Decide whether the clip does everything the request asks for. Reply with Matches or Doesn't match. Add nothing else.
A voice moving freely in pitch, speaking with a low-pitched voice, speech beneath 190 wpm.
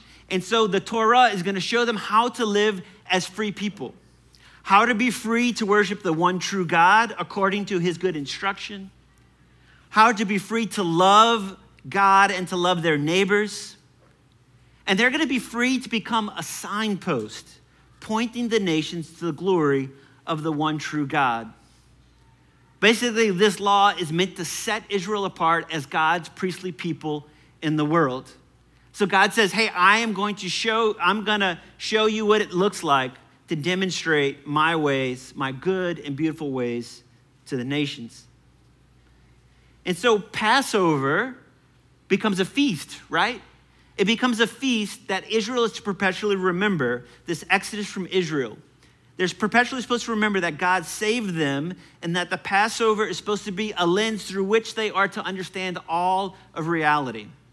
Doesn't match